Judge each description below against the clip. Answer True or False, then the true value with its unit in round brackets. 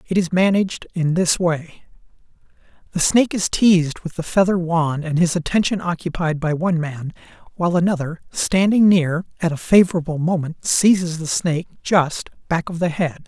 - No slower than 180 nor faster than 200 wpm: False (165 wpm)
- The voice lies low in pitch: False (170 Hz)